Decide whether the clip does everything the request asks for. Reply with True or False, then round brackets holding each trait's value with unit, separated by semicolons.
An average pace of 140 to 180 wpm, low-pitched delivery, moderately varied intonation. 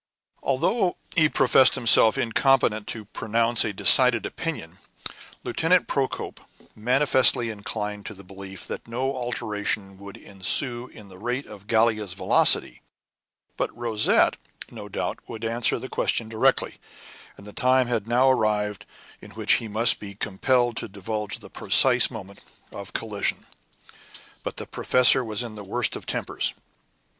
True (145 wpm; 115 Hz; 3.4 semitones)